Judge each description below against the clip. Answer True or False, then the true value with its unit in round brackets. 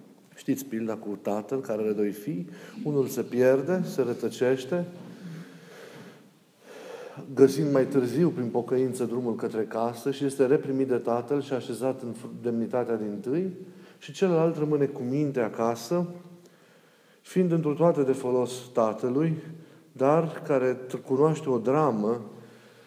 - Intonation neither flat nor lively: True (4.8 semitones)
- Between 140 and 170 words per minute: False (130 wpm)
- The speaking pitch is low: True (130 Hz)